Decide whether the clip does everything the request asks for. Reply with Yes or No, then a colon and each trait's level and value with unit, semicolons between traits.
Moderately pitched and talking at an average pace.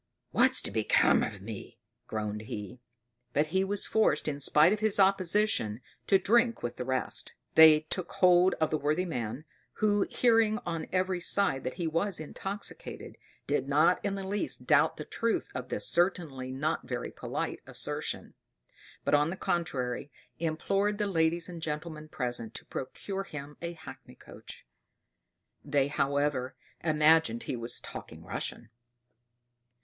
Yes: medium, 160 Hz; average, 150 wpm